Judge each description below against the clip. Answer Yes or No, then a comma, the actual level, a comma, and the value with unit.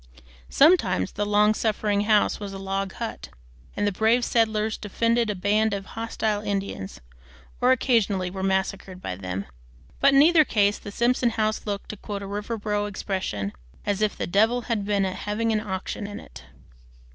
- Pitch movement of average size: No, narrow, 2.2 semitones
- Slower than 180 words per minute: Yes, average, 170 wpm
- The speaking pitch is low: No, high, 205 Hz